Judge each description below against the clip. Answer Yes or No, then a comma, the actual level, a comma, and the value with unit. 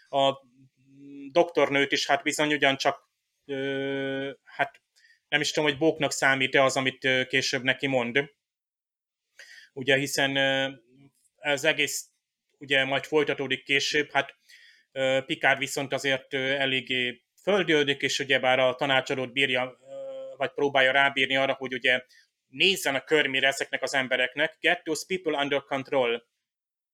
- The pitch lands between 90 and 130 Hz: No, medium, 140 Hz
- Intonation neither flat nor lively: No, narrow, 1.6 semitones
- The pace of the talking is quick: No, average, 125 wpm